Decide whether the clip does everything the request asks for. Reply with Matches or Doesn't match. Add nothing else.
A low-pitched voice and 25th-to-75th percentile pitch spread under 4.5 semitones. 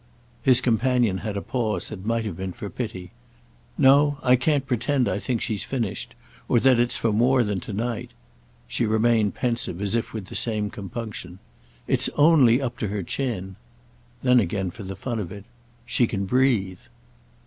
Matches